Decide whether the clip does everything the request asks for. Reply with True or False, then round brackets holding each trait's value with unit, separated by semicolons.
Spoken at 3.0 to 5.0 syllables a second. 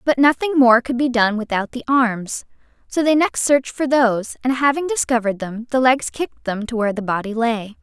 False (5.5 syllables/s)